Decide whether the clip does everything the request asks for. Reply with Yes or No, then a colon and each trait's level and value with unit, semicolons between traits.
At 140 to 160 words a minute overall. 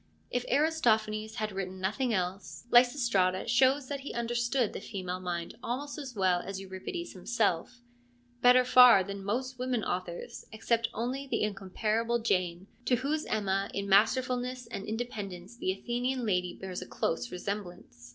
Yes: average, 150 wpm